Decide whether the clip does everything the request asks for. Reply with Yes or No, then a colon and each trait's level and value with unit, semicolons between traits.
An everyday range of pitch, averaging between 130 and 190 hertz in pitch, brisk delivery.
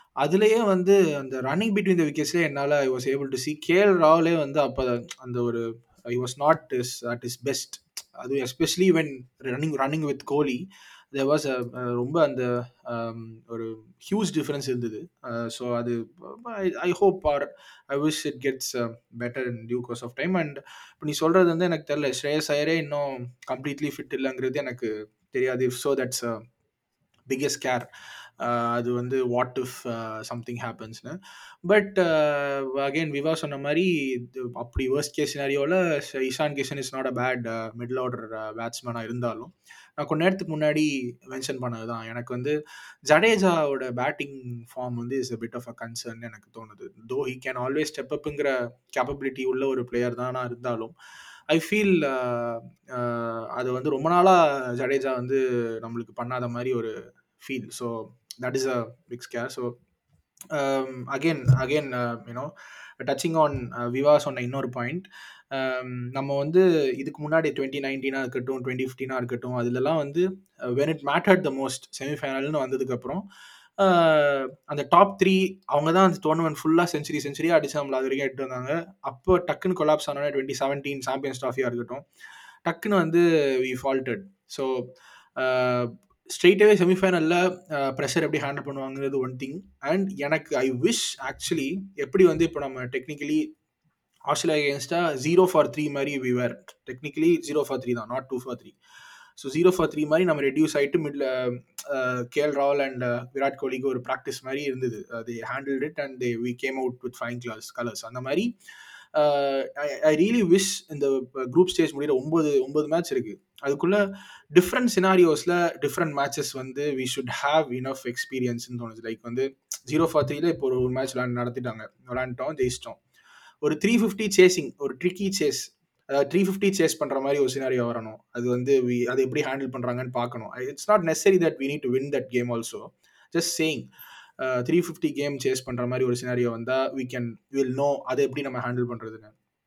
Yes: average, 4.1 semitones; low, 135 Hz; fast, 160 wpm